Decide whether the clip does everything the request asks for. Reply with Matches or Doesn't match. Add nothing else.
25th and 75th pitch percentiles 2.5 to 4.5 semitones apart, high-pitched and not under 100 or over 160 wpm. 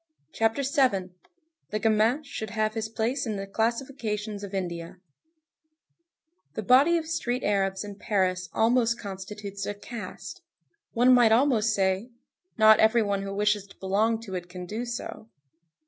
Matches